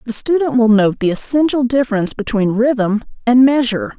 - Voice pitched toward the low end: No, high, 235 Hz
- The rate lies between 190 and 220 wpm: No, average, 165 wpm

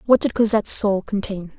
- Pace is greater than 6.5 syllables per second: No, 5.5 syllables/s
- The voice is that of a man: No, female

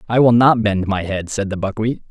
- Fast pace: Yes, fast, 255 wpm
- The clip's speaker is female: No, male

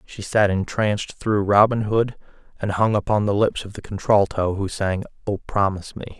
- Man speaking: Yes, male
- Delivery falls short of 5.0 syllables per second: No, 5.1 syllables/s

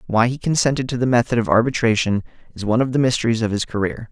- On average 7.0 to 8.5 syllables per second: Yes, 7.1 syllables/s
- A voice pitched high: No, low, 120 Hz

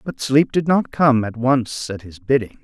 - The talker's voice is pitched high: No, low, 125 Hz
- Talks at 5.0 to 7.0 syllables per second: No, 4.4 syllables/s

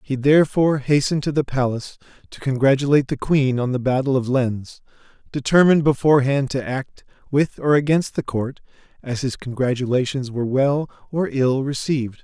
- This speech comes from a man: Yes, male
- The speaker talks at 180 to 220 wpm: No, average, 155 wpm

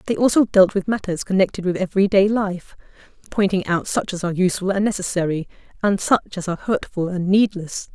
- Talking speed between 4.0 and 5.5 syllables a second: No, 6.0 syllables/s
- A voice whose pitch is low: No, high, 190 Hz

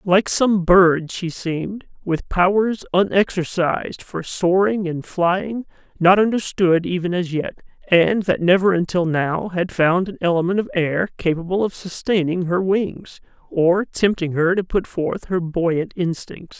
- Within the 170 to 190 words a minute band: No, average, 150 wpm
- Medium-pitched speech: Yes, medium, 180 Hz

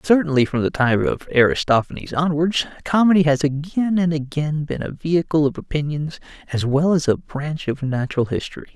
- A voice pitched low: No, medium, 150 Hz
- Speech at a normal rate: Yes, average, 170 wpm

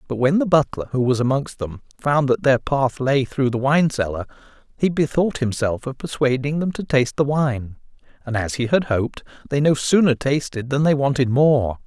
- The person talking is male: Yes, male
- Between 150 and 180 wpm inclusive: No, average, 200 wpm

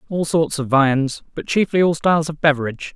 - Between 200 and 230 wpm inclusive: Yes, fast, 205 wpm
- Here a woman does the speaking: No, male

